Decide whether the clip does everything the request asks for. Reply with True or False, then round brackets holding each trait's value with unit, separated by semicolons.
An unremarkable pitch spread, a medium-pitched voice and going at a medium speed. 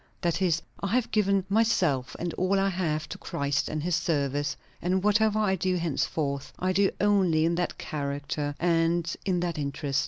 True (4.4 semitones; 170 Hz; 180 wpm)